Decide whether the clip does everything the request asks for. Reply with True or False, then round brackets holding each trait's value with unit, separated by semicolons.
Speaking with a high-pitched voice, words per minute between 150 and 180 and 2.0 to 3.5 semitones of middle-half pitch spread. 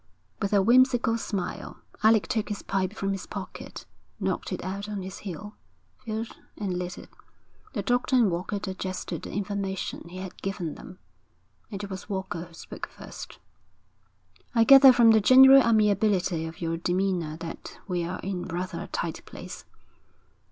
True (195 Hz; 160 wpm; 3.2 semitones)